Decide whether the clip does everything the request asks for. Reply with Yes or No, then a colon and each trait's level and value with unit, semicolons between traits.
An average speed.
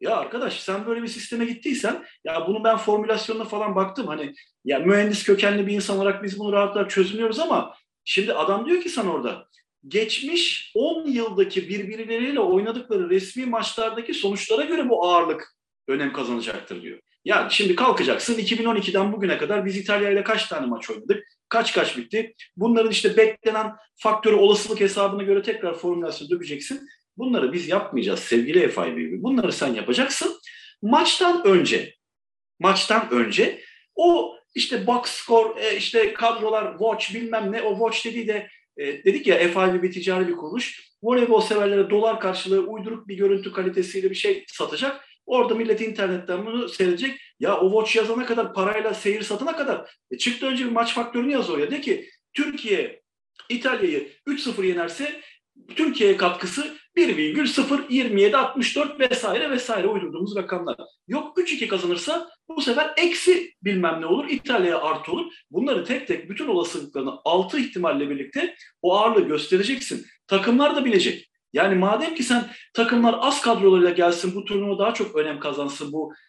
No: fast, 150 wpm